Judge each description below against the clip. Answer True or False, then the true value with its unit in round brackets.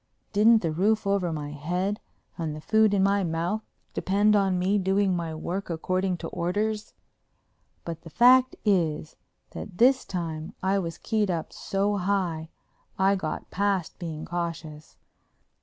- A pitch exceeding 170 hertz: True (185 Hz)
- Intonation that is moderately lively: True (3.5 semitones)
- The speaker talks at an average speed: True (155 wpm)